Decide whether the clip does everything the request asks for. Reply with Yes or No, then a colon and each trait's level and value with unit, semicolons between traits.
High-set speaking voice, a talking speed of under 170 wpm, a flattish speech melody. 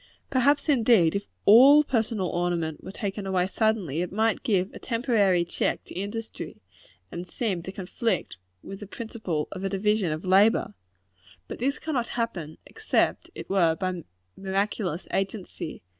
No: high, 195 Hz; average, 160 wpm; average, 4.1 semitones